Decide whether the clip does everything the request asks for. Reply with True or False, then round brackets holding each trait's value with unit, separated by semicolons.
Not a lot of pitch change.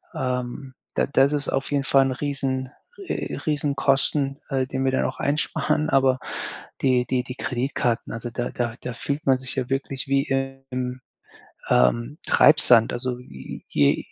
True (1.7 semitones)